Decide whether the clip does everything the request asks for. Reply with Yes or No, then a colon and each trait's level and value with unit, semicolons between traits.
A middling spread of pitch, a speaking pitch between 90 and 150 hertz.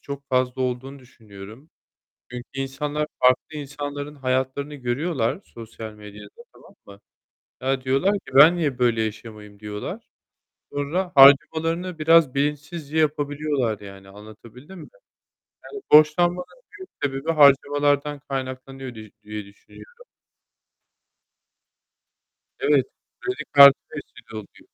Yes: average, 4.0 semitones; low, 135 Hz